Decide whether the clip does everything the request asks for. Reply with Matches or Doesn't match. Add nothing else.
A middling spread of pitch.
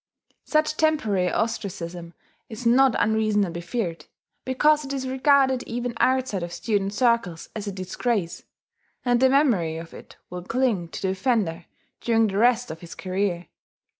Doesn't match